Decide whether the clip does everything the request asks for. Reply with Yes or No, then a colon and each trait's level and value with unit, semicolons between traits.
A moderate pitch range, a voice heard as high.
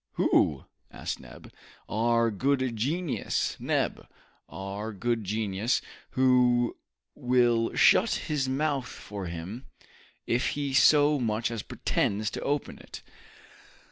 No: average, 3.7 semitones; low, 120 Hz